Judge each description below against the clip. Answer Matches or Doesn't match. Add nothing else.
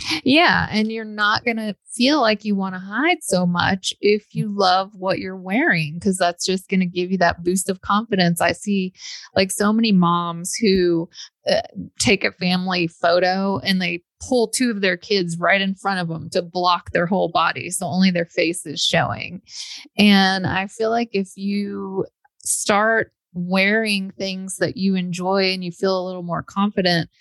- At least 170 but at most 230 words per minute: Matches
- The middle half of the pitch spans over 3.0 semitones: Doesn't match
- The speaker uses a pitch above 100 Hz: Matches